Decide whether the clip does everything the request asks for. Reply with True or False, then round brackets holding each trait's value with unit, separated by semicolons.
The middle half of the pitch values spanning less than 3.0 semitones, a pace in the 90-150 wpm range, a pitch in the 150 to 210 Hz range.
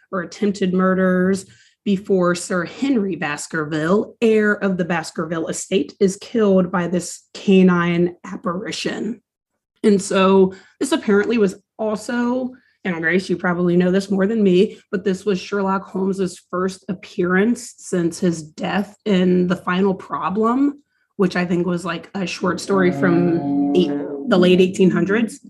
True (2.5 semitones; 140 wpm; 190 Hz)